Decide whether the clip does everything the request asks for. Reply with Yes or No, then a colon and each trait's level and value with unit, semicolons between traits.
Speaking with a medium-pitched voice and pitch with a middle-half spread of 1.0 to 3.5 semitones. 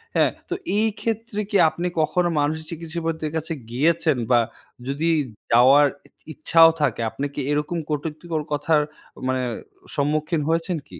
Yes: medium, 155 Hz; narrow, 2.4 semitones